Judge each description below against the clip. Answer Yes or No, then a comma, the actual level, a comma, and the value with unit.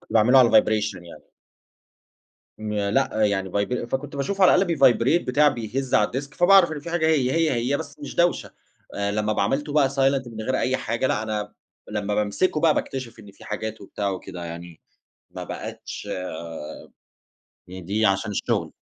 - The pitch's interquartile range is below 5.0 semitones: No, average, 5.3 semitones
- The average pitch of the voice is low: Yes, low, 120 Hz